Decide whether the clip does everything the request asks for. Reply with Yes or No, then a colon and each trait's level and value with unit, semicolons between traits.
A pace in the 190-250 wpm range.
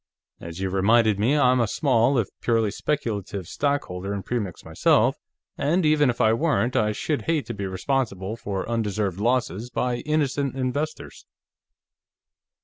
No: average, 145 wpm